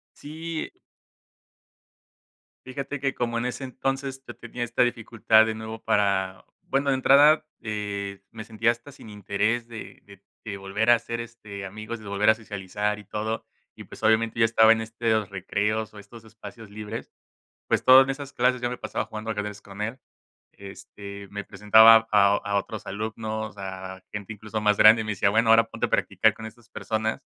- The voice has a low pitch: Yes, low, 110 Hz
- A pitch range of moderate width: No, narrow, 2.2 semitones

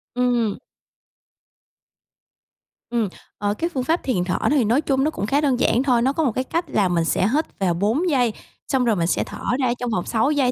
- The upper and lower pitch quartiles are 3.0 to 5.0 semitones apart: Yes, average, 4.7 semitones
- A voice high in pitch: Yes, high, 245 Hz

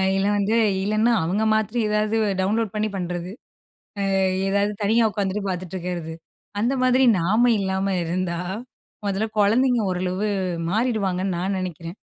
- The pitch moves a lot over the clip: No, average, 2.8 semitones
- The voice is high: Yes, high, 195 Hz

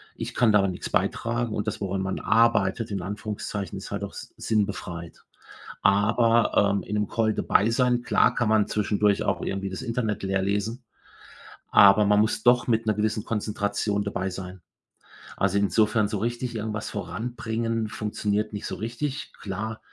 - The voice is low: Yes, low, 105 Hz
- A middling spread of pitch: No, narrow, 2.2 semitones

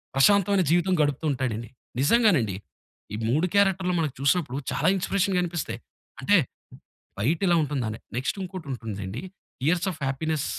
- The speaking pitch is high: No, medium, 155 Hz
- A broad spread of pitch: Yes, wide, 6.0 semitones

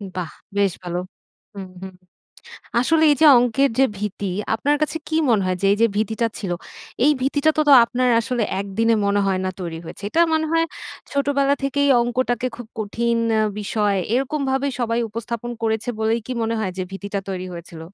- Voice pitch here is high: Yes, high, 230 Hz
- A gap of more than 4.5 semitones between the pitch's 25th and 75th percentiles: Yes, average, 5.2 semitones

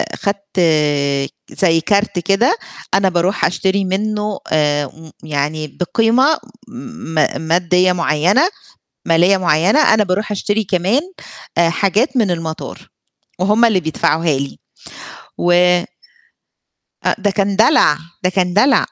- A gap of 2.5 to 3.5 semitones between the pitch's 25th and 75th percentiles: No, average, 4.0 semitones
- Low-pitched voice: No, medium, 185 Hz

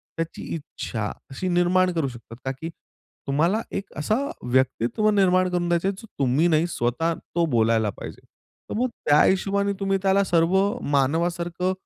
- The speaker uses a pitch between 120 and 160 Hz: No, medium, 170 Hz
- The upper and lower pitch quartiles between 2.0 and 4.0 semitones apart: No, wide, 5.4 semitones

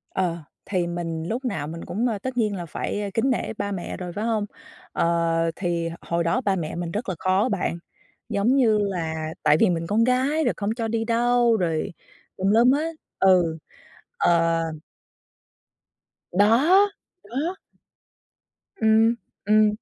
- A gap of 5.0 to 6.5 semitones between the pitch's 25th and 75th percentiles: Yes, wide, 5.4 semitones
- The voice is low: No, high, 205 Hz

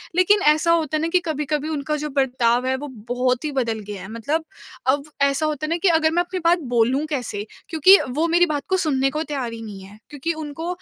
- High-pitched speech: Yes, very high, 295 Hz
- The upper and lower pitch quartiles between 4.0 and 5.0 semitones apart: Yes, average, 4.3 semitones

